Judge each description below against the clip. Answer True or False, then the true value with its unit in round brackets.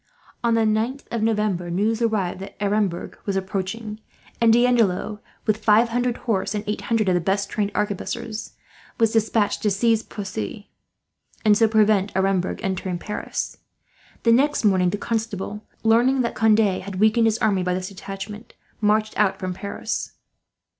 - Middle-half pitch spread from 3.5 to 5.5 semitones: False (2.6 semitones)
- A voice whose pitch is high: True (210 Hz)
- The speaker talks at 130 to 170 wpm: True (160 wpm)